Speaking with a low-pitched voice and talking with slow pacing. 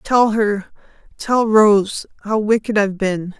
No: high, 210 Hz; slow, 105 wpm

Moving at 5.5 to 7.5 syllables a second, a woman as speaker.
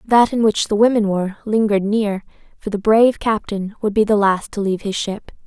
Yes: 5.6 syllables/s; female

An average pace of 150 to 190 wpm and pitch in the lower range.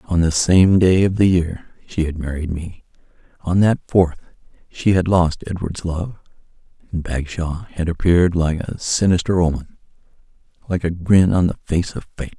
Yes: average, 165 wpm; very low, 85 Hz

